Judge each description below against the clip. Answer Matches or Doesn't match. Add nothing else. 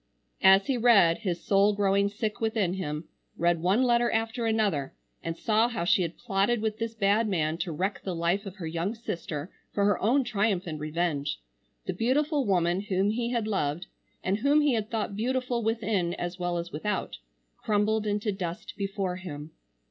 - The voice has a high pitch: Matches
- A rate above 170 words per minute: Matches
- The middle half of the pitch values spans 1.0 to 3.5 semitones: Doesn't match